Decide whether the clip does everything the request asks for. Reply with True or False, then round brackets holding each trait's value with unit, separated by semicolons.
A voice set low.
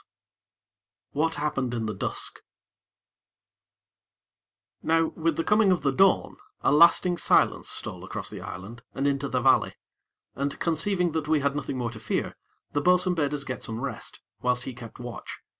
False (145 Hz)